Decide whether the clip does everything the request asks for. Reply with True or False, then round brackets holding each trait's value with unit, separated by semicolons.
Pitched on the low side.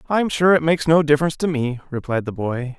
False (150 Hz)